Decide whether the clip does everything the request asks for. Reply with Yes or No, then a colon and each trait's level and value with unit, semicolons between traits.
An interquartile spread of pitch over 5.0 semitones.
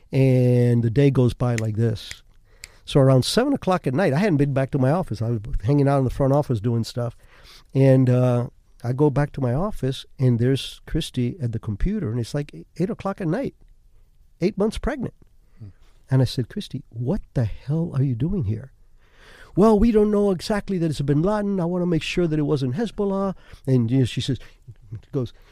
Yes: wide, 5.6 semitones